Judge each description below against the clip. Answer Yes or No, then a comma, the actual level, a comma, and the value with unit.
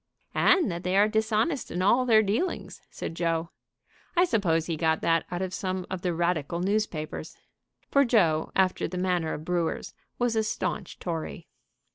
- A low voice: No, medium, 185 Hz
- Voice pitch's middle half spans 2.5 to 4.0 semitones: No, average, 4.5 semitones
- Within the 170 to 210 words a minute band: Yes, average, 175 wpm